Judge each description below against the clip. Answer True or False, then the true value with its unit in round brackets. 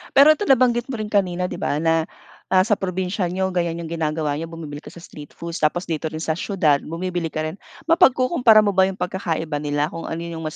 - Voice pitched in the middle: True (175 Hz)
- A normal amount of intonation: True (3.6 semitones)